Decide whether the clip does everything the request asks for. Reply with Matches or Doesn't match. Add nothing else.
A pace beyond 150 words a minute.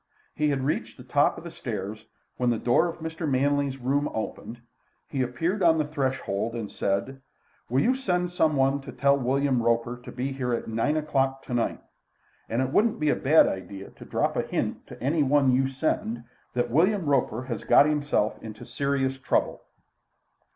Matches